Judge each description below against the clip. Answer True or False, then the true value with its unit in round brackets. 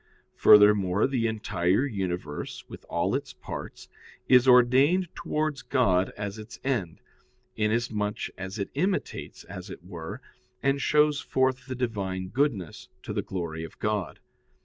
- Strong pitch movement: True (5.8 semitones)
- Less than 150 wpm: True (135 wpm)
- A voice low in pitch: True (105 Hz)